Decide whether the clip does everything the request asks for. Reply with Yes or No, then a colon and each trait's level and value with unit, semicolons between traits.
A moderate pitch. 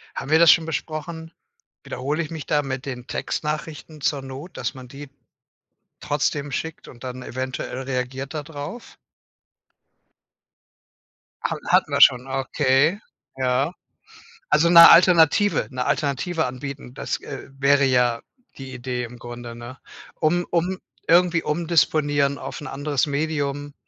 Yes: medium, 145 Hz